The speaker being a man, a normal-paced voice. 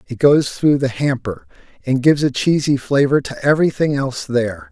Yes: male; average, 180 wpm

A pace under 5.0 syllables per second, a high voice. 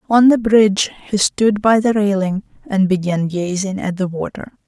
Yes: 4.8 syllables/s; high, 200 Hz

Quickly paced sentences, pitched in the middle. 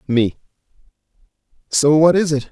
No: slow, 120 wpm; medium, 145 Hz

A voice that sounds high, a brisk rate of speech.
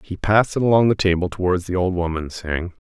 No: very low, 95 Hz; fast, 230 wpm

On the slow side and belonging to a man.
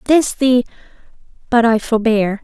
No: slow, 100 wpm; female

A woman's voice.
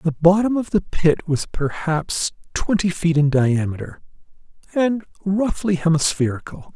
No: male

